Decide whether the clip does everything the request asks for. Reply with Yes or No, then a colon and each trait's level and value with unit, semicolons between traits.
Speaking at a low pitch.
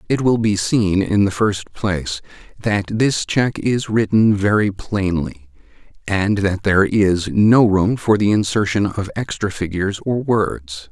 Yes: low, 100 Hz